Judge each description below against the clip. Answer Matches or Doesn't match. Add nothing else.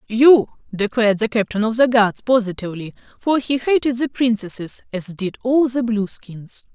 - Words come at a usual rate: Matches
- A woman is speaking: Matches